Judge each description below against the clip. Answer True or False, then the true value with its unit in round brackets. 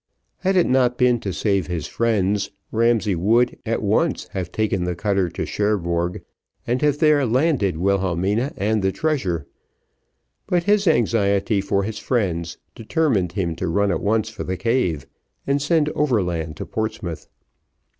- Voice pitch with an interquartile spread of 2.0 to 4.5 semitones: False (5.2 semitones)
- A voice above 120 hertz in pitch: False (105 Hz)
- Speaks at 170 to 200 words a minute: False (155 wpm)